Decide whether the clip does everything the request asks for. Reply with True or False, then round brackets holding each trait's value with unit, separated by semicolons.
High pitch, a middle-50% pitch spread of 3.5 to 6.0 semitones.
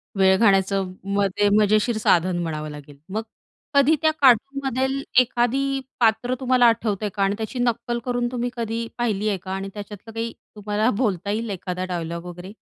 True (215 Hz; 3.9 semitones)